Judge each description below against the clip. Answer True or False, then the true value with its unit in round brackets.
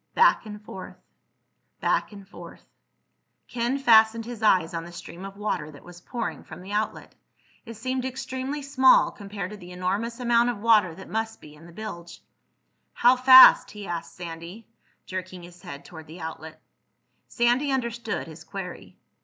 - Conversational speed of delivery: True (165 wpm)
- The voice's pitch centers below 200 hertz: False (205 Hz)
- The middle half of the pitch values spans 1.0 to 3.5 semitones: False (5.3 semitones)